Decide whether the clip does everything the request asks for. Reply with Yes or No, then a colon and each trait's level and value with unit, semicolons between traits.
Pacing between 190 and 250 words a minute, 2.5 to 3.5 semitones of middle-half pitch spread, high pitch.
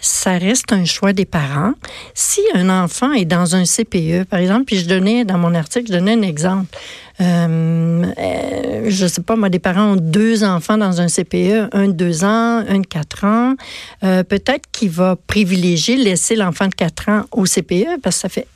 Yes: average, 205 wpm; average, 3.1 semitones; high, 195 Hz